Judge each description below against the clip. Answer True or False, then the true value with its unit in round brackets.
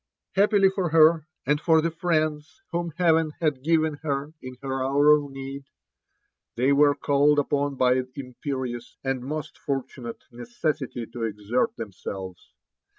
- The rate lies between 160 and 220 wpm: False (140 wpm)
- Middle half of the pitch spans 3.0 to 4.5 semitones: True (3.4 semitones)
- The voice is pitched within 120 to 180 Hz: True (140 Hz)